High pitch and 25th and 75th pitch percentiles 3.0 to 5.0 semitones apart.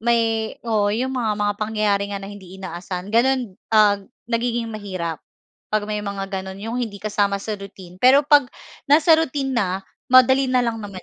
Yes: high, 215 Hz; average, 3.6 semitones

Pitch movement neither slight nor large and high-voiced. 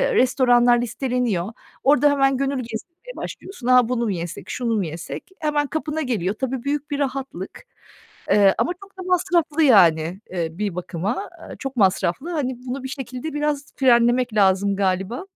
No: wide, 6.1 semitones; very high, 250 Hz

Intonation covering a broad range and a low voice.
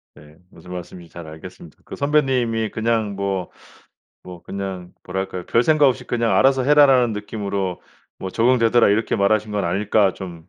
No: average, 4.5 semitones; low, 105 Hz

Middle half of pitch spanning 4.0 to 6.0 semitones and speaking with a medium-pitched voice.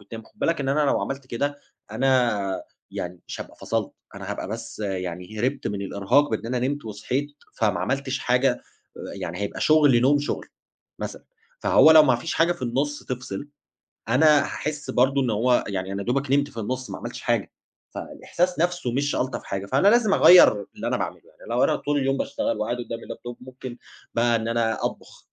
No: average, 4.4 semitones; low, 130 Hz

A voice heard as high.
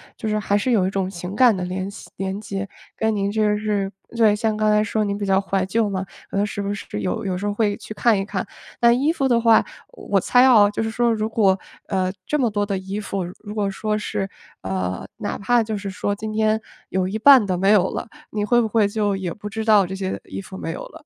Yes: high, 205 Hz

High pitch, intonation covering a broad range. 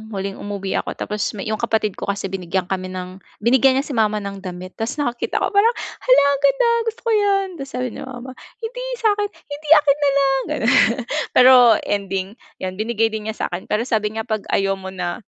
Yes: high, 220 Hz; wide, 6.3 semitones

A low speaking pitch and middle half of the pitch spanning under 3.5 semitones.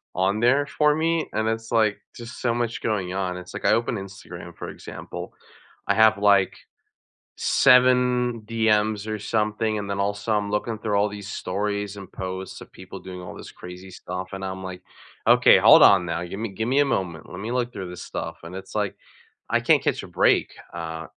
Yes: low, 105 Hz; average, 3.1 semitones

